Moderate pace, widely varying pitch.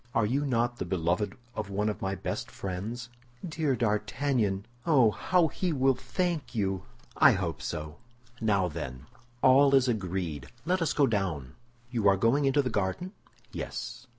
Yes: average, 160 wpm; wide, 5.9 semitones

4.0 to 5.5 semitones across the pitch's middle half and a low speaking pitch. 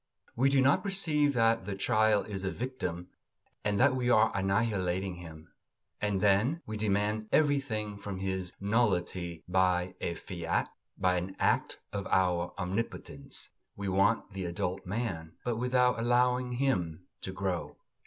Yes: average, 4.6 semitones; low, 100 Hz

